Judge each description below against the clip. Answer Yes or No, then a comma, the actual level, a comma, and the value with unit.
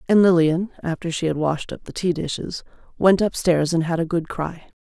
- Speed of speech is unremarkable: No, fast, 210 wpm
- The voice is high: No, medium, 170 Hz